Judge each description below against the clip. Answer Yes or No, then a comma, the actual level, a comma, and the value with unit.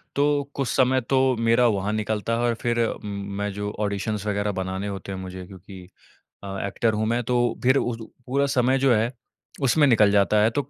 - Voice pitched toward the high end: No, low, 110 Hz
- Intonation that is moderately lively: Yes, average, 3.5 semitones